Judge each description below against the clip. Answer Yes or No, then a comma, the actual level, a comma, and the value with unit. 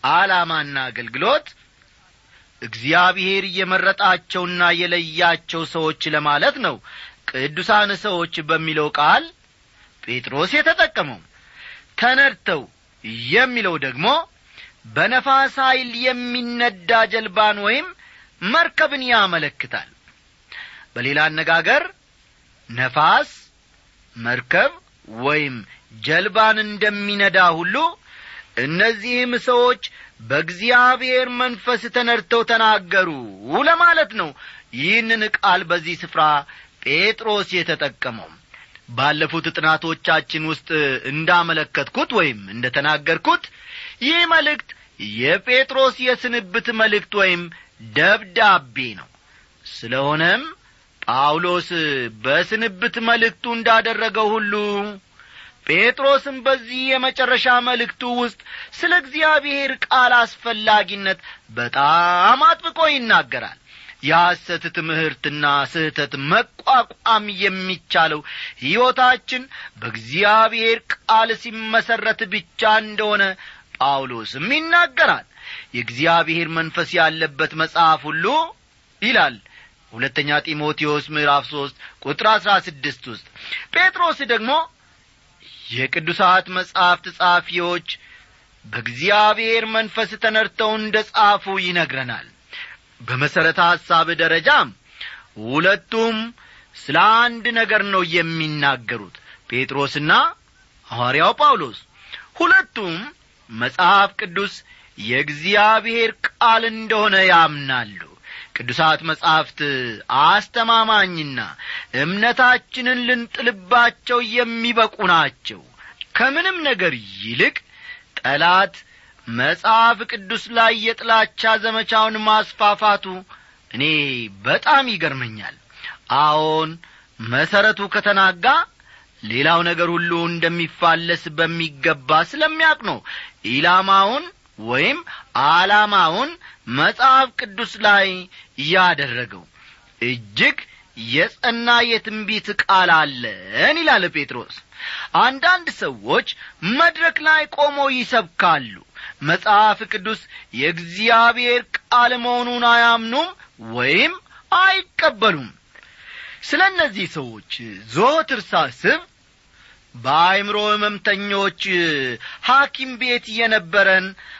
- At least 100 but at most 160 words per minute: No, average, 75 wpm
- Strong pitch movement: Yes, wide, 7.0 semitones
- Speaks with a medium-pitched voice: No, high, 205 Hz